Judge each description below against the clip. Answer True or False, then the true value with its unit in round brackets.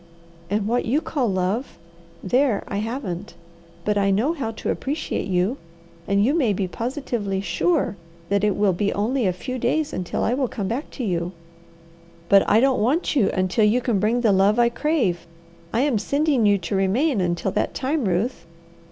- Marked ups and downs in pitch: False (5.0 semitones)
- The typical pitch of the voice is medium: False (215 Hz)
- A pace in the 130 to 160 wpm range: False (185 wpm)